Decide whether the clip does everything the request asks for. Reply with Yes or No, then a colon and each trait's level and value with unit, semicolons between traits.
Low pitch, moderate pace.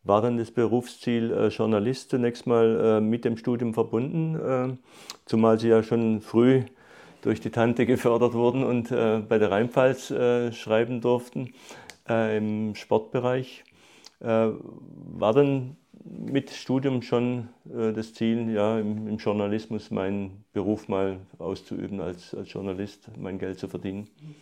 Yes: low, 115 Hz; average, 145 wpm